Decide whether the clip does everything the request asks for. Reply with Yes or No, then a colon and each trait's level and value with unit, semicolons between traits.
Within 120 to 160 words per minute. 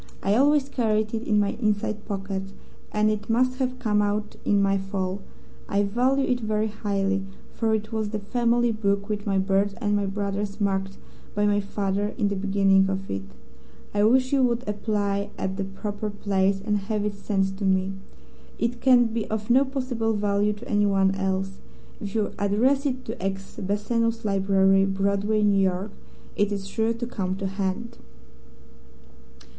No: average, 175 wpm